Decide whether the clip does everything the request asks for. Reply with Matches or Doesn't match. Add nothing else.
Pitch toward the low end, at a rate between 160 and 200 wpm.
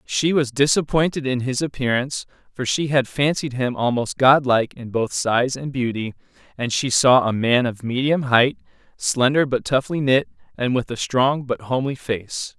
Matches